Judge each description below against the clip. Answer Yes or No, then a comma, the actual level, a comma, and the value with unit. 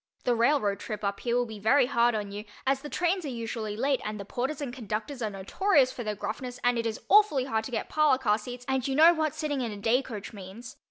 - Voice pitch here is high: Yes, high, 245 Hz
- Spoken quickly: Yes, fast, 260 wpm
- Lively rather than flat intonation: No, average, 4.2 semitones